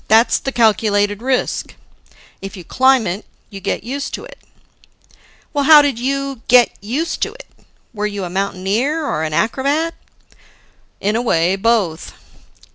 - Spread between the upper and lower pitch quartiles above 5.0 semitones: Yes, wide, 5.4 semitones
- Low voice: No, high, 230 Hz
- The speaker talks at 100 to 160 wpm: Yes, average, 145 wpm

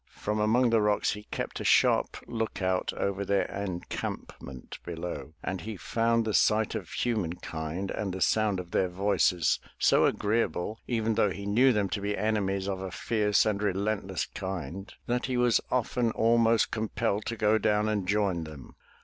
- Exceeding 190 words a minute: No, average, 175 wpm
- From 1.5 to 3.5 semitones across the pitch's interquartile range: Yes, average, 2.8 semitones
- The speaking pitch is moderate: No, low, 105 Hz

